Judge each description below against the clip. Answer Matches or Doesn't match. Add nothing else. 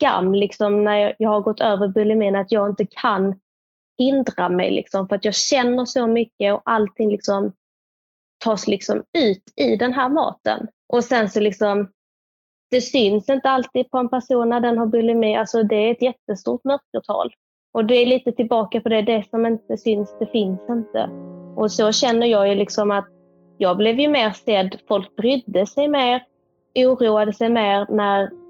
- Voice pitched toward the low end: Doesn't match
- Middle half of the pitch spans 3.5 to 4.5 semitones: Doesn't match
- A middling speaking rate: Matches